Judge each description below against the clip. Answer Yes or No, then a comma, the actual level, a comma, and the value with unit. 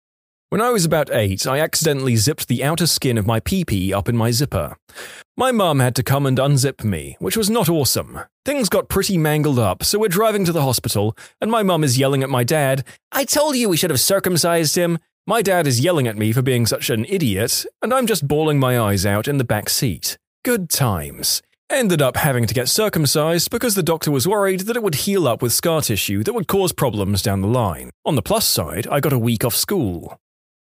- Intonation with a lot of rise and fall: Yes, wide, 7.7 semitones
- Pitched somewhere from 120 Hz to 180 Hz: Yes, medium, 140 Hz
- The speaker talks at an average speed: No, fast, 230 wpm